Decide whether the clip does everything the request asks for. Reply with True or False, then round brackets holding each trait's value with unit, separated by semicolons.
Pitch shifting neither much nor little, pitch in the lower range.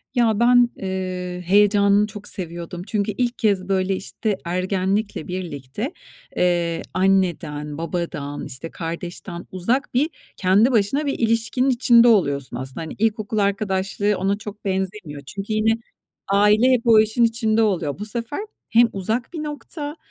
False (3.9 semitones; 200 Hz)